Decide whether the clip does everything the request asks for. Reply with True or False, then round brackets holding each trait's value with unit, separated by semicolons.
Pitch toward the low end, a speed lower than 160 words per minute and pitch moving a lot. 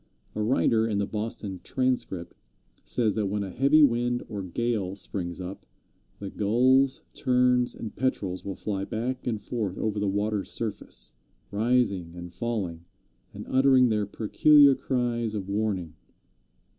False (110 Hz; 145 wpm; 4.0 semitones)